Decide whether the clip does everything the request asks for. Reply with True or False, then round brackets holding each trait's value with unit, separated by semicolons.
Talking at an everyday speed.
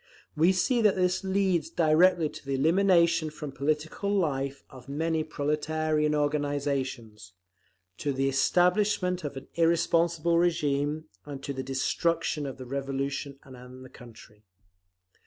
False (130 wpm)